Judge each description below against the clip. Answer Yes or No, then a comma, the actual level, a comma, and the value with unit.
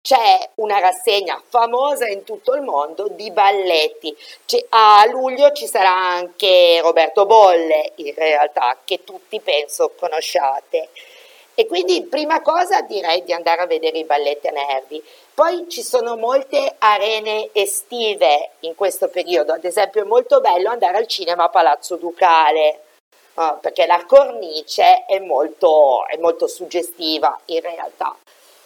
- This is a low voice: No, high, 200 Hz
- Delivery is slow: No, average, 140 wpm